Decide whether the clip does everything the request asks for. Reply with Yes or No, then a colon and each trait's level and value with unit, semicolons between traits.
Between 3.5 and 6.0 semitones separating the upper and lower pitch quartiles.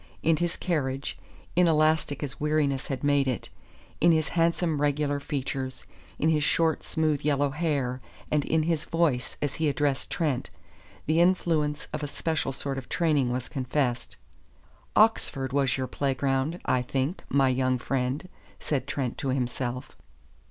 No: average, 3.0 semitones